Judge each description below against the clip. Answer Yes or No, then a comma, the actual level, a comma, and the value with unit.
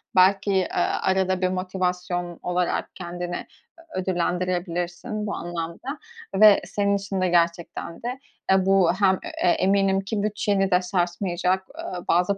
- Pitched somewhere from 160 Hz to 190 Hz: Yes, medium, 185 Hz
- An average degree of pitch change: No, narrow, 1.8 semitones